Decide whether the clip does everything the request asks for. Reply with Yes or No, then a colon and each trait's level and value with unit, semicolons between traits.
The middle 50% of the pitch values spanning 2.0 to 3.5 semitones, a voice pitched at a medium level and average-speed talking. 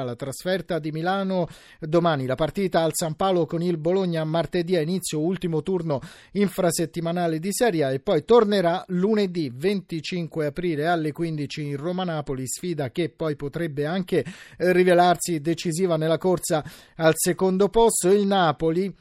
Yes: average, 2.7 semitones; medium, 170 Hz; average, 145 wpm